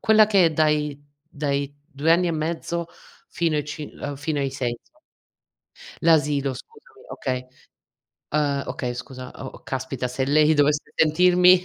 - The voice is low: No, medium, 150 Hz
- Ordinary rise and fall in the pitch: Yes, average, 3.1 semitones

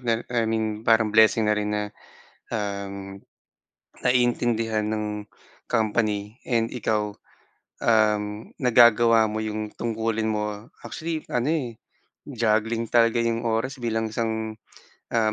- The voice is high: No, low, 110 Hz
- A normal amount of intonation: No, narrow, 1.5 semitones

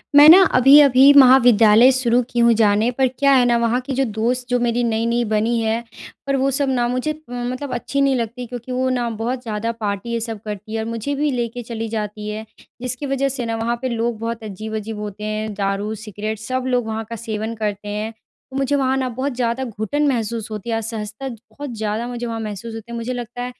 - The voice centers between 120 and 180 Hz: No, high, 235 Hz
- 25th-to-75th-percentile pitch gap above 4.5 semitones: No, narrow, 2.6 semitones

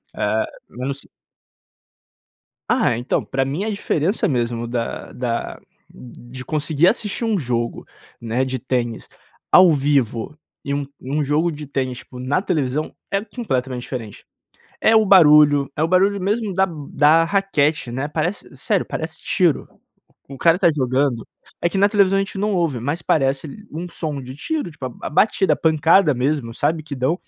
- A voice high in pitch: No, medium, 150 Hz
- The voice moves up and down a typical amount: No, wide, 5.9 semitones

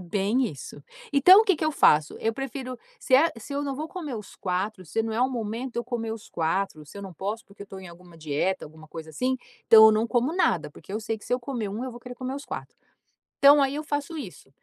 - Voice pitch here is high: Yes, high, 225 Hz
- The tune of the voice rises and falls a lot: Yes, wide, 5.7 semitones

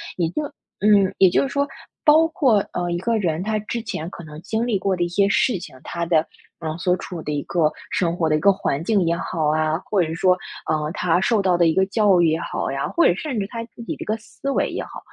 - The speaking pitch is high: No, medium, 180 Hz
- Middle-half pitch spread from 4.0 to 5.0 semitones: Yes, average, 4.6 semitones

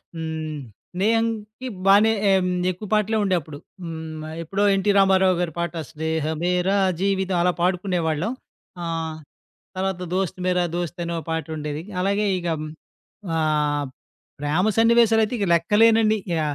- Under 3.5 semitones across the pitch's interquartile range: No, average, 4.3 semitones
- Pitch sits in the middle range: Yes, medium, 180 Hz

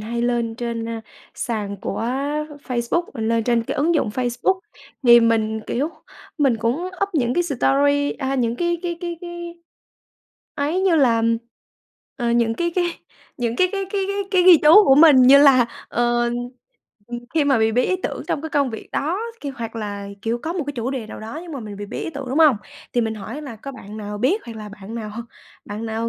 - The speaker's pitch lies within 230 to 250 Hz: Yes, high, 245 Hz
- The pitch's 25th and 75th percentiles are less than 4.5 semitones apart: No, average, 5.2 semitones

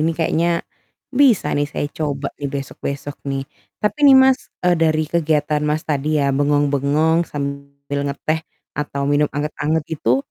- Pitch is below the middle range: No, medium, 150 Hz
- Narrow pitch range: Yes, narrow, 2.3 semitones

